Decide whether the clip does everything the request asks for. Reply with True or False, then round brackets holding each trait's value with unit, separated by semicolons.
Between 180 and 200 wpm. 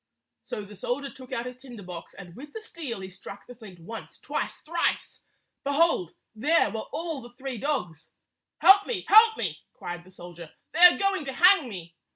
True (190 wpm)